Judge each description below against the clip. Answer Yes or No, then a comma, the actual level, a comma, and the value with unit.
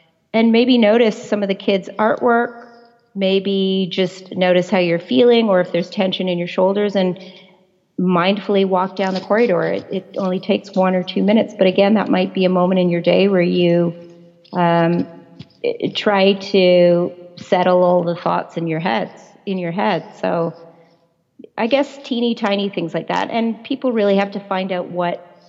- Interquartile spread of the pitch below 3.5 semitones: Yes, narrow, 2.6 semitones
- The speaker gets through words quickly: No, average, 180 wpm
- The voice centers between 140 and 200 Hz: Yes, high, 190 Hz